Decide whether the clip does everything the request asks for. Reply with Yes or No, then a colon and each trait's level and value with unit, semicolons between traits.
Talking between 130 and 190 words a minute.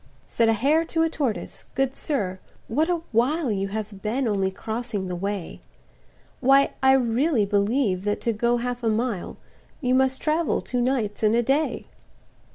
Yes: average, 170 wpm